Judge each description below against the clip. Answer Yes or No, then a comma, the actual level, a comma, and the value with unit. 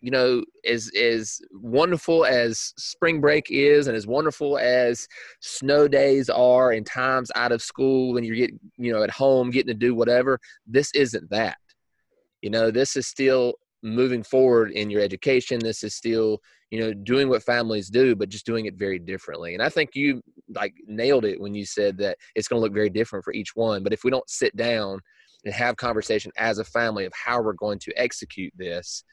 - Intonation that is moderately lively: Yes, average, 3.1 semitones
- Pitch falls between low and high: No, low, 120 Hz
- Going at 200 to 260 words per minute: Yes, fast, 205 wpm